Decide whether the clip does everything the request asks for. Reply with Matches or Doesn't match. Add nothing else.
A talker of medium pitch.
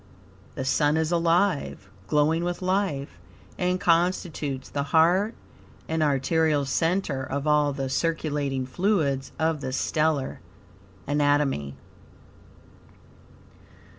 Matches